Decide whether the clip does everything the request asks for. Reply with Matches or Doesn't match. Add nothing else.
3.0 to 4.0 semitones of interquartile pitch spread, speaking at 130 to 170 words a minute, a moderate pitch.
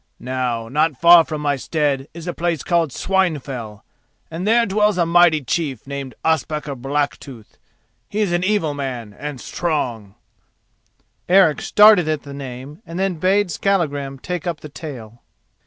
Doesn't match